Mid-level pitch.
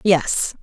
Yes: medium, 175 Hz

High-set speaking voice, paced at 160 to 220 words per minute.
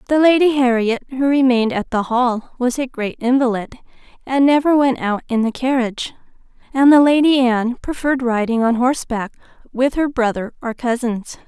Yes: very high, 250 Hz; average, 165 wpm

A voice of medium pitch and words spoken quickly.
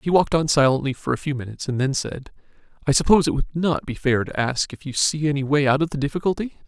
Yes: medium, 145 Hz; fast, 260 wpm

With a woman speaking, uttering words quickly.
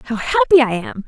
Yes: female; fast, 225 wpm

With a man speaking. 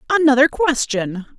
No: female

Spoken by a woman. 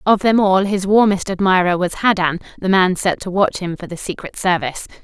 Yes: female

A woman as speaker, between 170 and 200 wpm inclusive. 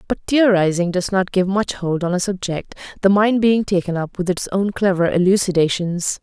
Yes: female; average, 195 wpm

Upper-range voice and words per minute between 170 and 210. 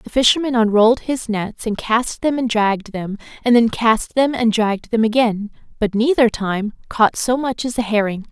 Yes: high, 225 Hz; average, 200 wpm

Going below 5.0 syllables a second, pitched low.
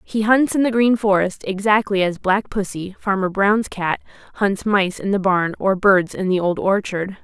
No: 4.5 syllables/s; high, 195 Hz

